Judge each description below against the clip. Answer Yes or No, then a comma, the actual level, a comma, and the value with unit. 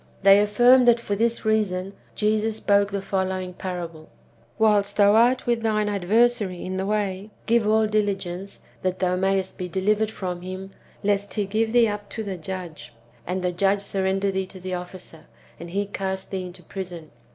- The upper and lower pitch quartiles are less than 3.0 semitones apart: Yes, narrow, 2.4 semitones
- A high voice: Yes, high, 195 Hz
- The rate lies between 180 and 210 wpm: Yes, average, 185 wpm